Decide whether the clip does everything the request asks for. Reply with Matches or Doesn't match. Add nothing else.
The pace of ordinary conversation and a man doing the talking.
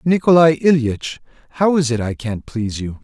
Matches